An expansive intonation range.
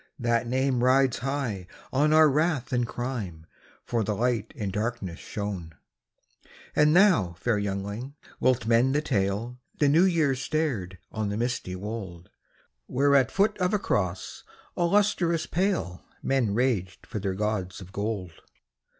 Yes: wide, 5.9 semitones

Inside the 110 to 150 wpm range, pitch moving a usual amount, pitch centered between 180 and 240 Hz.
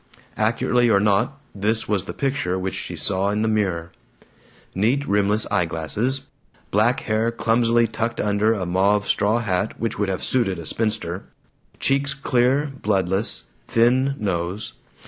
No: average, 145 wpm; average, 3.3 semitones; low, 105 Hz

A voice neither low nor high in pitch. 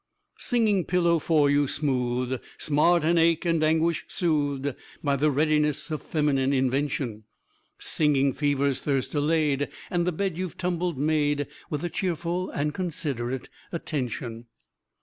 Yes: medium, 150 Hz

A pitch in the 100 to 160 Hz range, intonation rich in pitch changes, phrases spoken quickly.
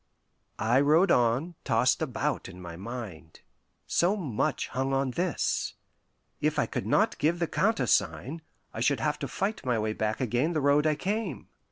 No: low, 135 Hz; wide, 6.1 semitones; average, 170 wpm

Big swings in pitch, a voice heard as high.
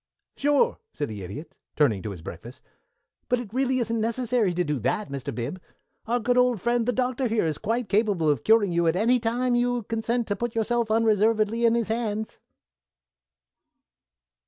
No: average, 4.8 semitones; high, 225 Hz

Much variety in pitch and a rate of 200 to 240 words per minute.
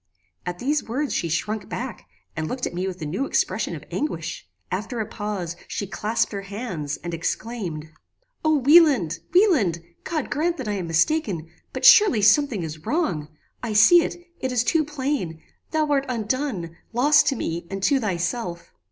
No: wide, 8.5 semitones; average, 175 wpm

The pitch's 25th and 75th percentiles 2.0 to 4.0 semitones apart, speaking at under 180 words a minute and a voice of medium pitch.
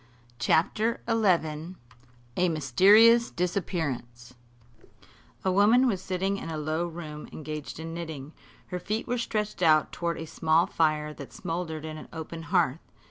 Yes: average, 3.6 semitones; average, 140 wpm; medium, 165 Hz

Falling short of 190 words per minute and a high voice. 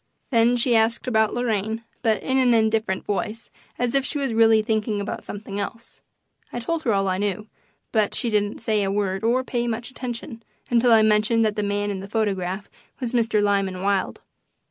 No: average, 195 wpm; high, 220 Hz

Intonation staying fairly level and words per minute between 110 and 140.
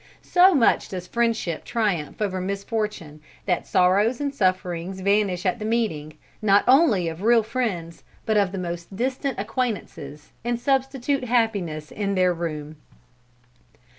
No: average, 5.0 semitones; slow, 135 wpm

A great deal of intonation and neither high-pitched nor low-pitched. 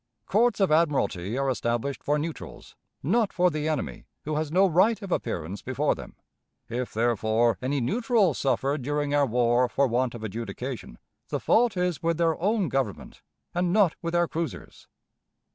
Yes: wide, 6.5 semitones; medium, 145 Hz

